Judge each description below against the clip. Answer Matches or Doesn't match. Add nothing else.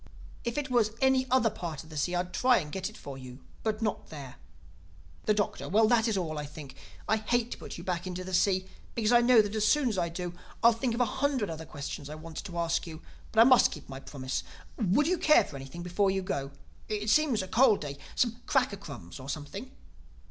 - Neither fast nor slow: Doesn't match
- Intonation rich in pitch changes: Matches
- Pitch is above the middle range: Matches